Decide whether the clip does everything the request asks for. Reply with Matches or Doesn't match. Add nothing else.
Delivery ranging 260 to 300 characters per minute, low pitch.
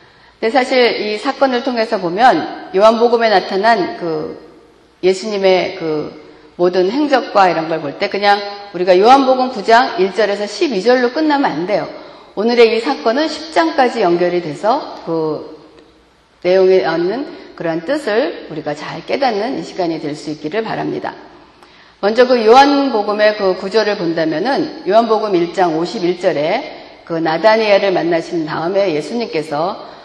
Doesn't match